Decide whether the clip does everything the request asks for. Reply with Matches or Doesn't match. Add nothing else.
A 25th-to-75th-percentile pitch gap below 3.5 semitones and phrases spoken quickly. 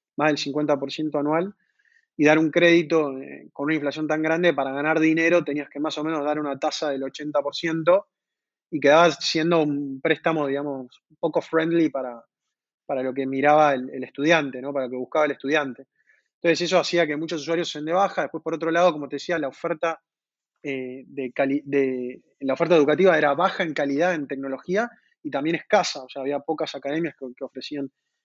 Matches